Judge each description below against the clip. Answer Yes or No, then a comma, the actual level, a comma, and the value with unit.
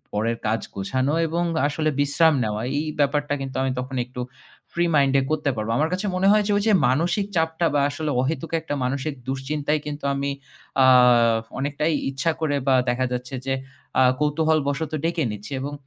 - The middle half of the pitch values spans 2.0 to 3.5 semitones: Yes, average, 3.2 semitones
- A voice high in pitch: No, medium, 145 Hz